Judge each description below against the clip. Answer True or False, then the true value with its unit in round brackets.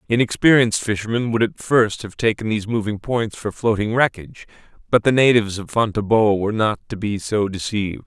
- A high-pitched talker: False (110 Hz)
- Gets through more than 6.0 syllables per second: False (5.8 syllables/s)